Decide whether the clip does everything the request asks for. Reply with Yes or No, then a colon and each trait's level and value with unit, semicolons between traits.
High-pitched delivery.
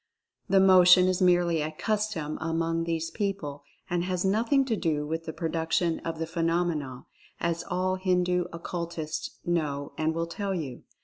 No: medium, 170 Hz